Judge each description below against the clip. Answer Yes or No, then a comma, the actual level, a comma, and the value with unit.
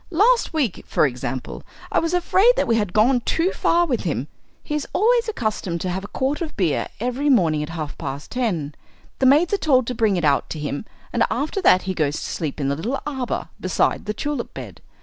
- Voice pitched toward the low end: No, high, 230 Hz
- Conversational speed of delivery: No, fast, 225 wpm